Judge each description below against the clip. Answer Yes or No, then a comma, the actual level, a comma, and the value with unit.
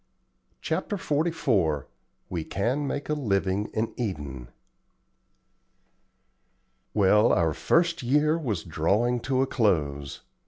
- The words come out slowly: Yes, slow, 105 wpm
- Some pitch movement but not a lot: No, wide, 8.9 semitones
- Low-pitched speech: Yes, low, 110 Hz